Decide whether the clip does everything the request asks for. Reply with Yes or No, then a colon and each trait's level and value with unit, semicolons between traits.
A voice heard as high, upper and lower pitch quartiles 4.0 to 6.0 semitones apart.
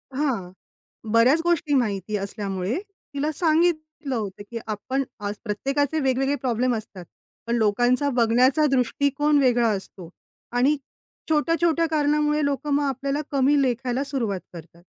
Yes: very high, 265 Hz; average, 4.6 semitones